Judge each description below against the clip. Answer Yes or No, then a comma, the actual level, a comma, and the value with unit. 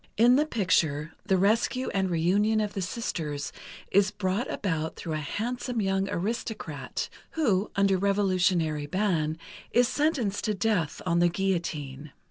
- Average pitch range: Yes, average, 4.4 semitones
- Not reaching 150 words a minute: Yes, average, 140 wpm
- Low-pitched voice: No, high, 195 Hz